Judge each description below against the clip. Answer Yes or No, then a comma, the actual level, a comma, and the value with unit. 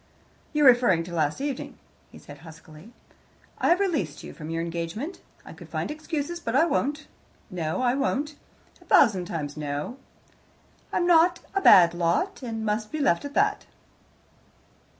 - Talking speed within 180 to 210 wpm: No, average, 155 wpm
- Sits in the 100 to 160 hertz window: No, high, 230 Hz